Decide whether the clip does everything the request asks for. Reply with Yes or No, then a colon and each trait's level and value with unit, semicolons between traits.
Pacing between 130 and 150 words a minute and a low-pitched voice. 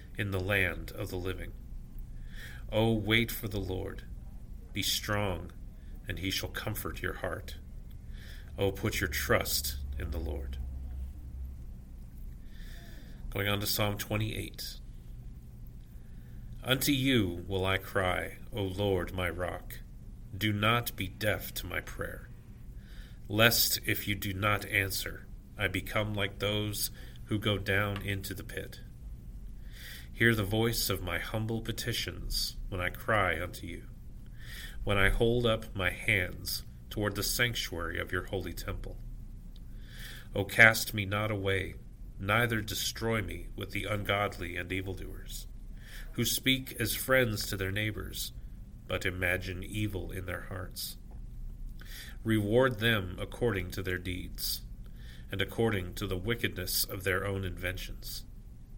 Yes: slow, 135 wpm; low, 100 Hz